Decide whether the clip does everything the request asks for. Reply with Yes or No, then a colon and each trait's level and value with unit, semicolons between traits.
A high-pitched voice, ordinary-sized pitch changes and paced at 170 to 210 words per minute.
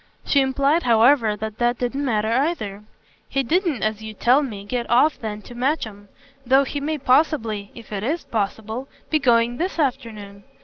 Yes: high, 240 Hz; average, 4.3 semitones; average, 175 wpm